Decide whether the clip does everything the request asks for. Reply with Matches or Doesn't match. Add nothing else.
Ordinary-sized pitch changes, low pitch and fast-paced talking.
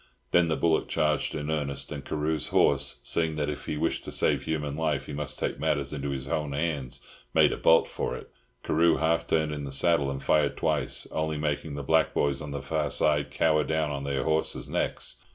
Doesn't match